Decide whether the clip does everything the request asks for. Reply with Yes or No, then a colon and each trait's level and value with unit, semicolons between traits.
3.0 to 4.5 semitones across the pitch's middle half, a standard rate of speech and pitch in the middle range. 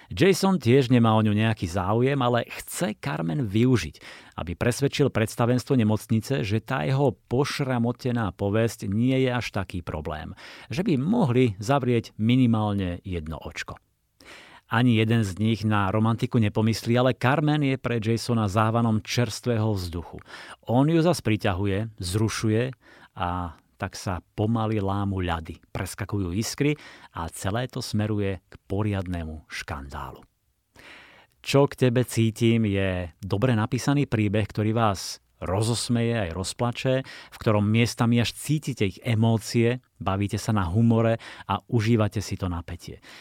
No: average, 3.5 semitones; average, 130 wpm; low, 110 Hz